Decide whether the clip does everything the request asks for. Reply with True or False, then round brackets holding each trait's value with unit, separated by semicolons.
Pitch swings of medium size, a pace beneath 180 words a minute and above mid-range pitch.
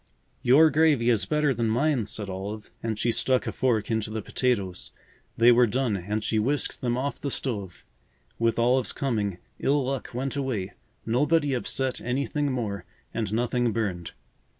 False (3.8 semitones; 165 wpm; 120 Hz)